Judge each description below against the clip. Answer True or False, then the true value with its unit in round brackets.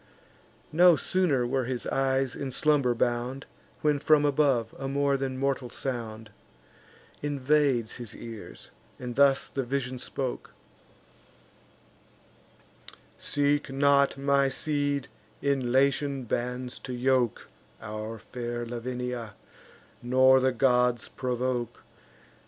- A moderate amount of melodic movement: False (2.3 semitones)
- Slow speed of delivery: True (105 wpm)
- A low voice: True (130 Hz)